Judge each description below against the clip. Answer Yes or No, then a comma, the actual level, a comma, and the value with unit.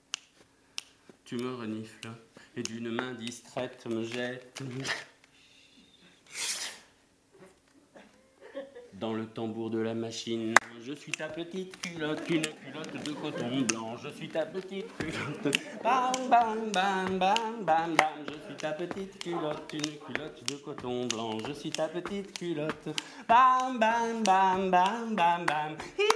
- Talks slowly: Yes, slow, 130 wpm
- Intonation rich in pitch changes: Yes, wide, 7.5 semitones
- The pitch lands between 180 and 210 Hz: No, medium, 155 Hz